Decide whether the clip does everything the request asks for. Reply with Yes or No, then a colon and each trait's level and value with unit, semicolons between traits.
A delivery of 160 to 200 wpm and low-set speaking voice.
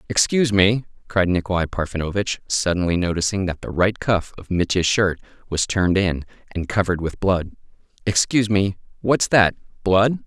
No: average, 150 wpm; very low, 95 Hz